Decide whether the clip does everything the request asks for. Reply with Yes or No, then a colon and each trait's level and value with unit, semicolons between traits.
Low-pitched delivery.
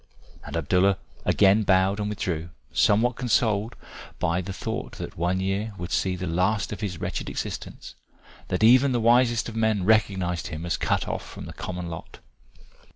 Yes: low, 100 Hz